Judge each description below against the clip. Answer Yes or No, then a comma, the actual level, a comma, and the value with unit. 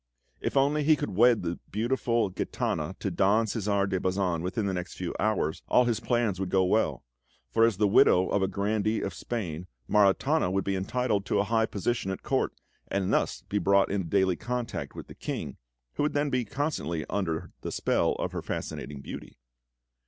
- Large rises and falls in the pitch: No, average, 3.8 semitones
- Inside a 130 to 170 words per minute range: No, average, 195 wpm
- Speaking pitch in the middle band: No, low, 100 Hz